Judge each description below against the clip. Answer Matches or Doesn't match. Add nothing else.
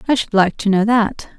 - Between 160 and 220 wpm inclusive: Doesn't match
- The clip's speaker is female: Matches